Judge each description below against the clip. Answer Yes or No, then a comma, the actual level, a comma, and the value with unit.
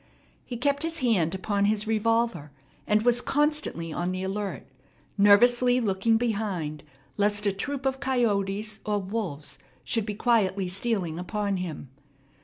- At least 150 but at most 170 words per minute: No, average, 140 wpm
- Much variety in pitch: No, average, 3.8 semitones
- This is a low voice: No, high, 210 Hz